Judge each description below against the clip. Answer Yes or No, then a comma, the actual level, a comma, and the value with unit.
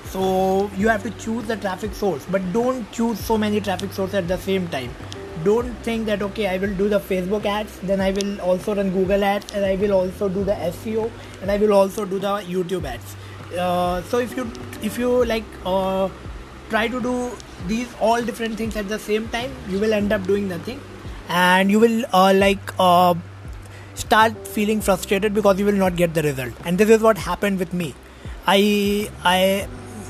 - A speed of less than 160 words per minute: No, average, 200 wpm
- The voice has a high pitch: Yes, high, 200 Hz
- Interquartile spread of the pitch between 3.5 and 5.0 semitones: No, average, 2.7 semitones